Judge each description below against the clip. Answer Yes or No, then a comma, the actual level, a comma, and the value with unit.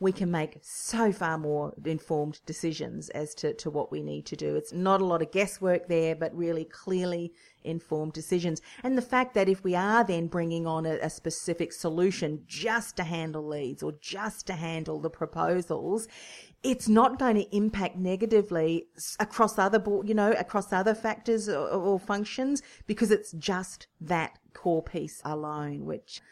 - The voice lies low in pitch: No, medium, 175 Hz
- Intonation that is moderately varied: Yes, average, 4.5 semitones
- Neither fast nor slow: Yes, average, 175 wpm